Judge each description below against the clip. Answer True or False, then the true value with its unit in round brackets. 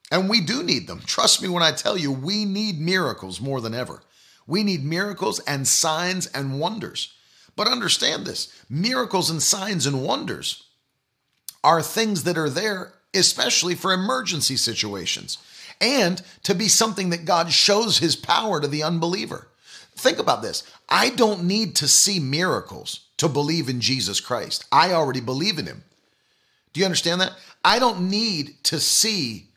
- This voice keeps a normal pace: True (165 wpm)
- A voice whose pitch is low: False (170 Hz)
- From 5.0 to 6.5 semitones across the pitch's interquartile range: True (5.4 semitones)